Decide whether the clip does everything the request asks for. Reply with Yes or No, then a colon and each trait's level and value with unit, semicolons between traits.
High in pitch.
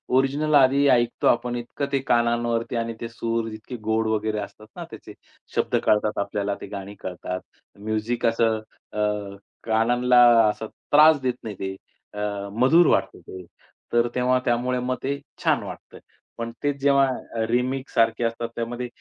No: low, 115 Hz